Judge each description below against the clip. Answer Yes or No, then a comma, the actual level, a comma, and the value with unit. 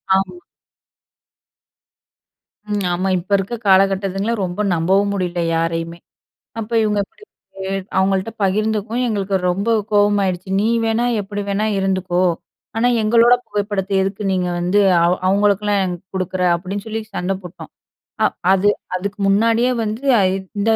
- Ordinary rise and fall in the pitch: No, narrow, 2.0 semitones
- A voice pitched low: No, high, 195 Hz